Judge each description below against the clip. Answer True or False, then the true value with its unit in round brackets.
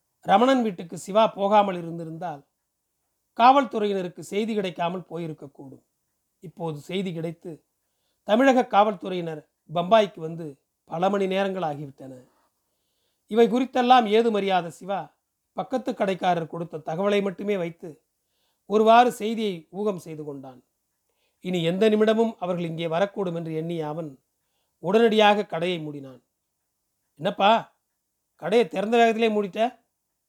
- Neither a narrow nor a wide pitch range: True (4.6 semitones)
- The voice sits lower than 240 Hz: True (190 Hz)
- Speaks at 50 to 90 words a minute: False (105 wpm)